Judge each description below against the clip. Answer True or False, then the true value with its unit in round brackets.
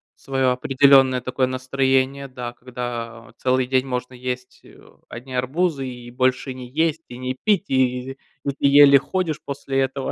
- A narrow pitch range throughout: True (1.5 semitones)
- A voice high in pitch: False (130 Hz)